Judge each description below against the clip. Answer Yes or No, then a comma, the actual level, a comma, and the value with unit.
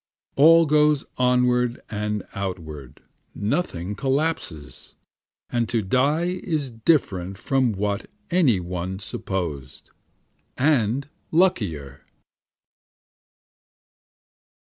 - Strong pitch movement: Yes, wide, 7.4 semitones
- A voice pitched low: Yes, low, 115 Hz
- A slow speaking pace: Yes, slow, 80 wpm